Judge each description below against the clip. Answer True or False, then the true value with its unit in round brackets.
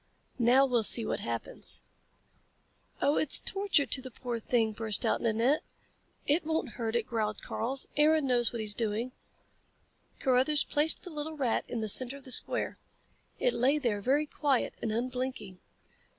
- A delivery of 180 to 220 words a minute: False (165 wpm)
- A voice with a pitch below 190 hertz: False (250 Hz)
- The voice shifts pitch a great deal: False (4.1 semitones)